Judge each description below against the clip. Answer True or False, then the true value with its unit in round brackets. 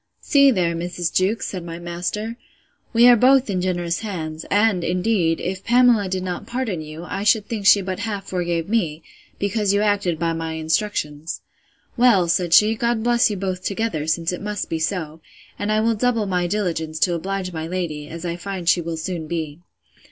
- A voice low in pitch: False (185 Hz)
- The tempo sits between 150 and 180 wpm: False (190 wpm)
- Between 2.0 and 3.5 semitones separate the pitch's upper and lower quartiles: False (3.9 semitones)